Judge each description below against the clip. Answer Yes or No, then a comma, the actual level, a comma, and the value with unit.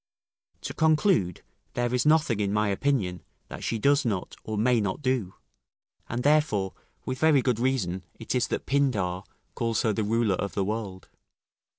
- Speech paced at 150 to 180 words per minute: Yes, average, 170 wpm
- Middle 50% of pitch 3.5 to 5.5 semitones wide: Yes, average, 4.8 semitones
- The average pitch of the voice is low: Yes, low, 115 Hz